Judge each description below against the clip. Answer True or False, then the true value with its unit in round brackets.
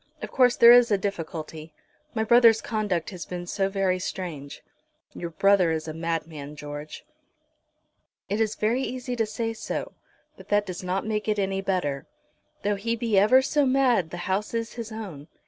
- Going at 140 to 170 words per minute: False (180 wpm)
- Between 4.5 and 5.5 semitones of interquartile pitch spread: True (5.0 semitones)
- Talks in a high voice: True (195 Hz)